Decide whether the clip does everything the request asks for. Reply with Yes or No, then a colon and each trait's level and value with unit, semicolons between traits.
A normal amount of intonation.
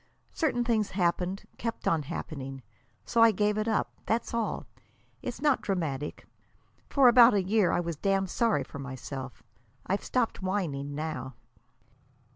No: wide, 7.4 semitones